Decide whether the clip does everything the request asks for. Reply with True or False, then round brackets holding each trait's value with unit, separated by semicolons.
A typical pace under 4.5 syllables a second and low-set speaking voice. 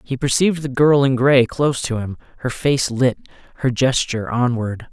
False (5.1 syllables/s; 130 Hz)